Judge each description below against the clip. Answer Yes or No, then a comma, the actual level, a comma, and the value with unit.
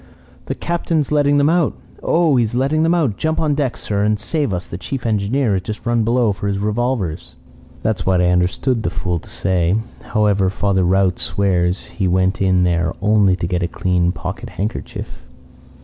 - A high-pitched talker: No, low, 105 Hz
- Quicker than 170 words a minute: Yes, average, 195 wpm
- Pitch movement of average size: No, wide, 5.7 semitones